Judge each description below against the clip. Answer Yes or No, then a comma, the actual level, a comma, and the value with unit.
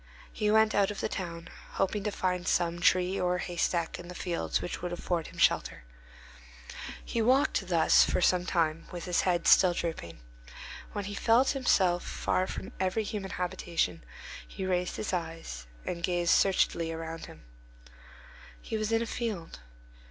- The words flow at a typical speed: Yes, average, 165 wpm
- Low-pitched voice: No, medium, 180 Hz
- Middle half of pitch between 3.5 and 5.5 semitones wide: No, average, 2.8 semitones